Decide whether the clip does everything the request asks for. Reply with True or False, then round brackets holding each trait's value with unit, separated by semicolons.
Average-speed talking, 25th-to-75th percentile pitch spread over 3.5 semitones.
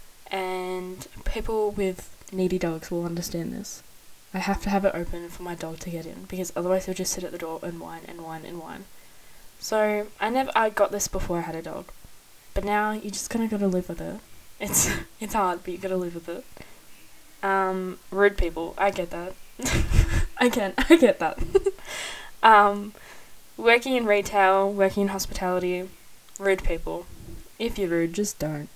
False (190 wpm; 3.0 semitones)